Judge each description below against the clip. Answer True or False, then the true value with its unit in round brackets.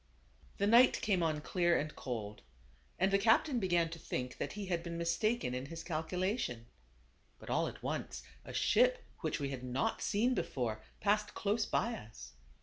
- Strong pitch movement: True (7.1 semitones)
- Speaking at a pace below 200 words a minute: True (180 wpm)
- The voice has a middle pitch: True (170 Hz)